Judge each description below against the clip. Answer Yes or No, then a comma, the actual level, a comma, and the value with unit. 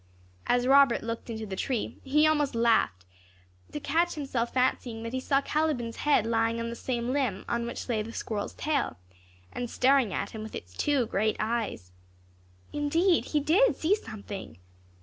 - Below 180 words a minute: Yes, average, 170 wpm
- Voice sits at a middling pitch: No, high, 240 Hz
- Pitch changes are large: No, average, 4.2 semitones